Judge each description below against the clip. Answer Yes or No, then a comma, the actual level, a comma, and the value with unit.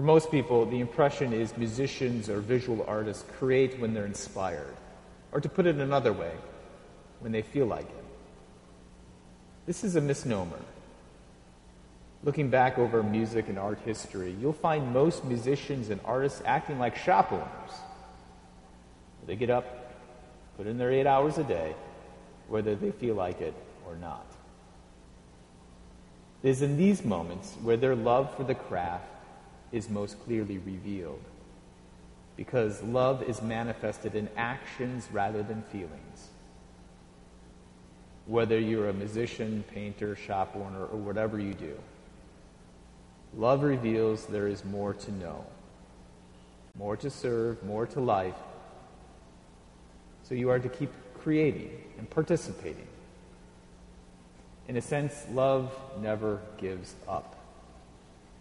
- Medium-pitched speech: No, low, 105 Hz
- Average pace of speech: No, slow, 130 wpm